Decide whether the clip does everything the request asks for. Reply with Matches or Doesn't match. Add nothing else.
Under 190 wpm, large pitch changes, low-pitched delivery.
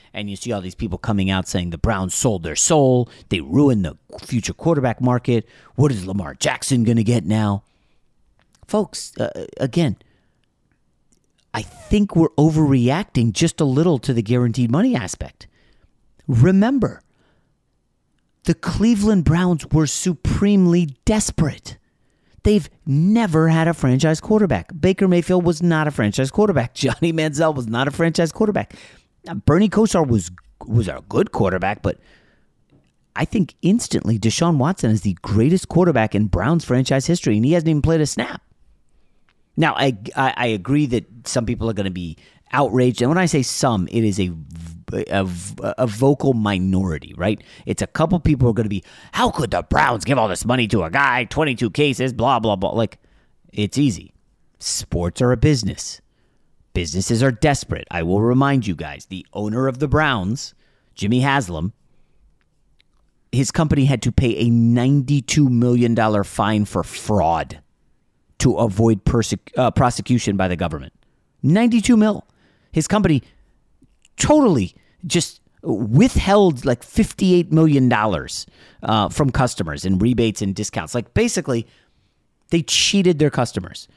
Matches